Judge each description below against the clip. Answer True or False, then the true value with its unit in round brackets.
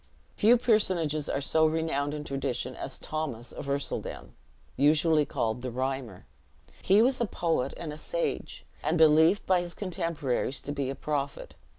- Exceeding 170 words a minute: False (160 wpm)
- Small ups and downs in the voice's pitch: False (3.8 semitones)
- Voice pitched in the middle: True (150 Hz)